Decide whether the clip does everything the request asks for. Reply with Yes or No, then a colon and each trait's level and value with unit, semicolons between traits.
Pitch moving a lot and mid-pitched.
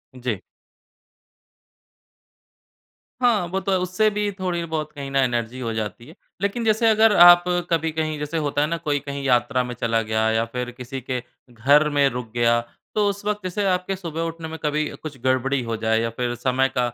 Yes: wide, 6.1 semitones; medium, 145 Hz